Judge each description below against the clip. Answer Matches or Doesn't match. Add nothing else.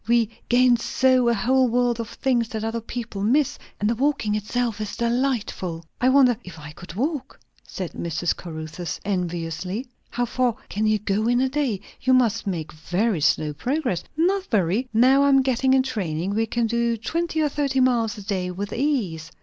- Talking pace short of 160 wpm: Doesn't match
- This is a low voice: Doesn't match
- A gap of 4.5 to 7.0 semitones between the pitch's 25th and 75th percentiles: Matches